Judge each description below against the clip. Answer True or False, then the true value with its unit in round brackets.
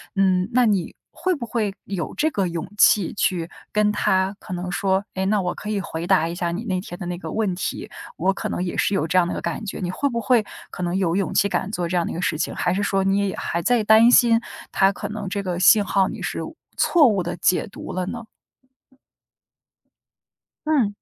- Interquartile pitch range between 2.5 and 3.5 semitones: True (2.9 semitones)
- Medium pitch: False (195 Hz)